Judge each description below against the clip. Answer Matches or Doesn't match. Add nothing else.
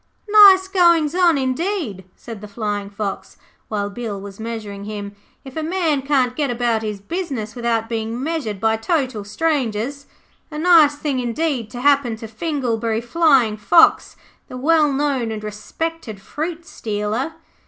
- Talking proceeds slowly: Doesn't match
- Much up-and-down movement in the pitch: Matches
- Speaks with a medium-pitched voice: Doesn't match